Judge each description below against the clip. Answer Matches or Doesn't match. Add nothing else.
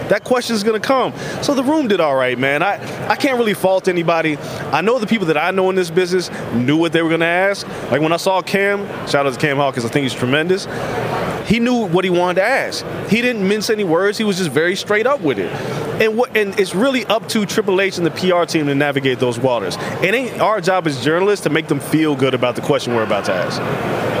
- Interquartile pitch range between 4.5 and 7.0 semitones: Matches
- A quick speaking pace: Matches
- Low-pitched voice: Doesn't match